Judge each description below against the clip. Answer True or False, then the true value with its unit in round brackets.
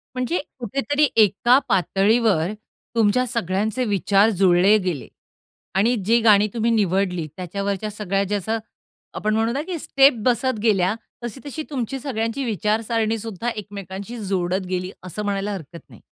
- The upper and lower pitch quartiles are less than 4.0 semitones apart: True (3.3 semitones)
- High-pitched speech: True (210 Hz)